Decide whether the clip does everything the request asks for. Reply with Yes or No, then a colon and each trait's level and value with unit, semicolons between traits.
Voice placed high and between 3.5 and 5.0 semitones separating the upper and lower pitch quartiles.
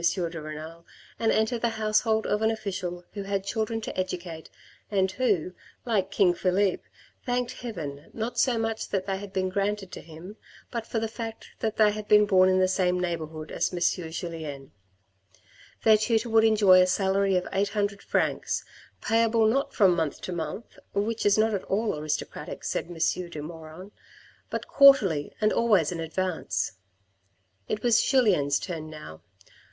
Yes: high, 195 Hz; average, 4.2 semitones